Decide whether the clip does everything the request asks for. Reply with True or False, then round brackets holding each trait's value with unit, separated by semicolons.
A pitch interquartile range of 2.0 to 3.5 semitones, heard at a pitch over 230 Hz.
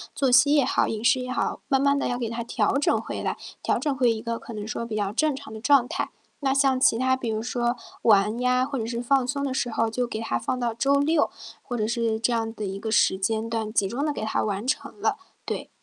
True (3.2 semitones; 240 Hz)